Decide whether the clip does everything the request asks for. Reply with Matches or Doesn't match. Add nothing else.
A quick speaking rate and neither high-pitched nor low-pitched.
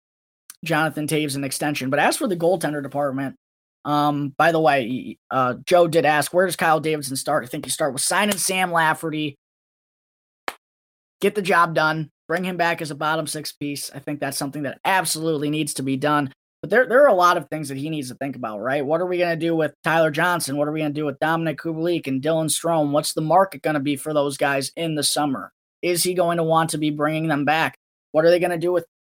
Matches